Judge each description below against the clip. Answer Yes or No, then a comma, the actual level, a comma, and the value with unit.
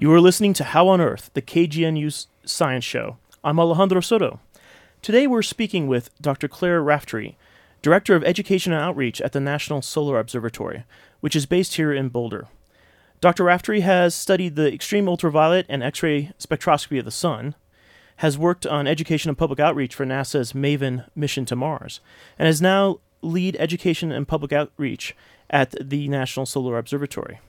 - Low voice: No, medium, 155 Hz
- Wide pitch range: No, average, 4.0 semitones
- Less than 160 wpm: No, average, 165 wpm